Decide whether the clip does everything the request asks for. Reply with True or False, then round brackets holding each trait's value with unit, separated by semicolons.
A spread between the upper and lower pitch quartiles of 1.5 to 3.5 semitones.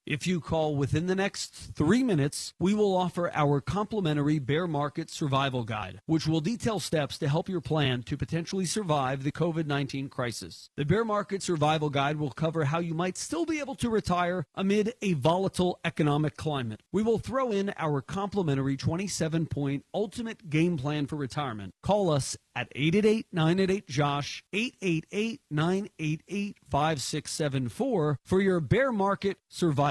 False (4.8 semitones)